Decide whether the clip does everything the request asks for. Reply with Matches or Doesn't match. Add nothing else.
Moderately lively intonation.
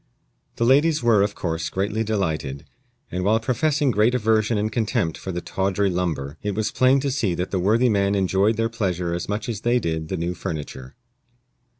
Matches